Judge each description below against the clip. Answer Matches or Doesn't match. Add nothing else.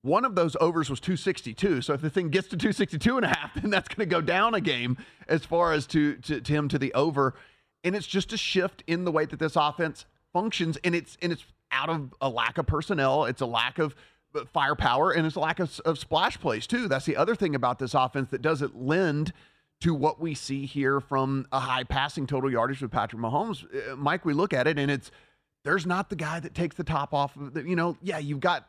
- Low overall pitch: Doesn't match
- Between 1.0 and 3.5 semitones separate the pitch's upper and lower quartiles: Doesn't match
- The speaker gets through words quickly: Matches